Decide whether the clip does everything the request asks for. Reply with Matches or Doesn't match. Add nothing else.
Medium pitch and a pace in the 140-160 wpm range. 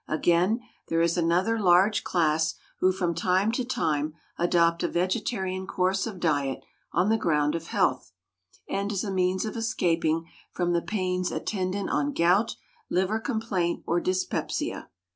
Matches